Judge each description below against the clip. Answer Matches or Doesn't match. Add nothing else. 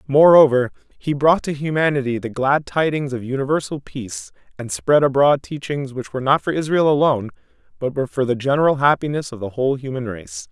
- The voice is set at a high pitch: Doesn't match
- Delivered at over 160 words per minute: Matches